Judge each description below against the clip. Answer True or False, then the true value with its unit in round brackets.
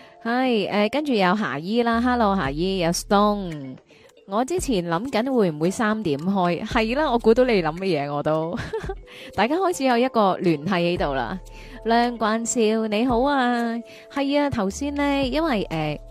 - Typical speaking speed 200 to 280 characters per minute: True (265 characters per minute)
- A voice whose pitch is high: True (220 Hz)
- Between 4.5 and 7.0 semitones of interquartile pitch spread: True (5.3 semitones)